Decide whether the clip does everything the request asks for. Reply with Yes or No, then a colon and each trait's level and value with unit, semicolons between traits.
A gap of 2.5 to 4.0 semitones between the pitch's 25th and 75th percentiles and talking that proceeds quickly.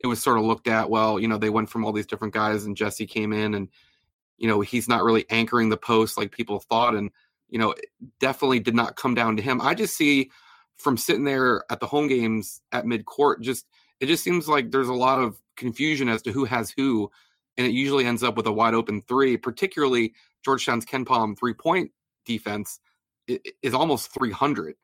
Yes: average, 3.2 semitones; fast, 220 wpm